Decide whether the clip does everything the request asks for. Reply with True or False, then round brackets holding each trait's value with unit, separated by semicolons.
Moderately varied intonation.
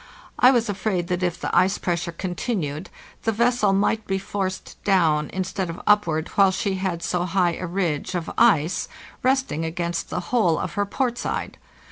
True (3.2 semitones)